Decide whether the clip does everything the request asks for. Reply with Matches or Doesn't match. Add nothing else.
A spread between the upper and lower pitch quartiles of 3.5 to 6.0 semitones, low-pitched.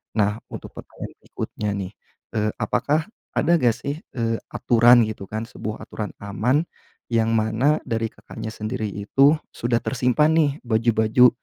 Doesn't match